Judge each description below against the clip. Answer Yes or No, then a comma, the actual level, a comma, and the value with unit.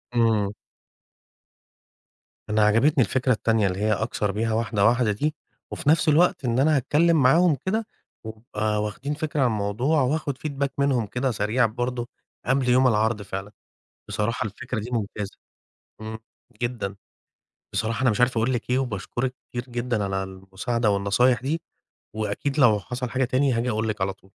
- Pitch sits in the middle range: No, low, 120 Hz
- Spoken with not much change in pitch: No, average, 3.7 semitones